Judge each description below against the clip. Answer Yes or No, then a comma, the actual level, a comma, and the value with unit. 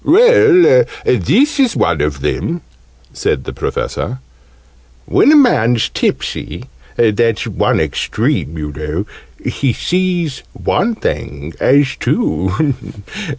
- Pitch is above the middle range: No, low, 130 Hz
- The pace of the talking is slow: Yes, slow, 110 wpm